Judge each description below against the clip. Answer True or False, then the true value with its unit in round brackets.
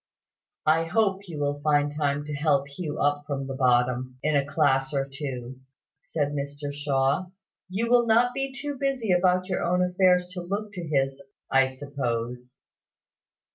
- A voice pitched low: False (145 Hz)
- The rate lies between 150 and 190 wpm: True (165 wpm)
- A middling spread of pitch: True (5.0 semitones)